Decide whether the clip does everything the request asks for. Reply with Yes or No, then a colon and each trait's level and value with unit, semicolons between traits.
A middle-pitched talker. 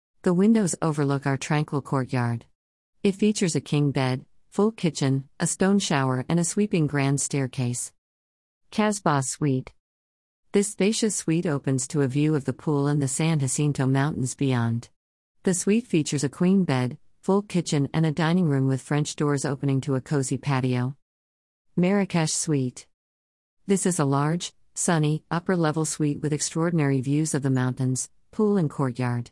Yes: medium, 145 Hz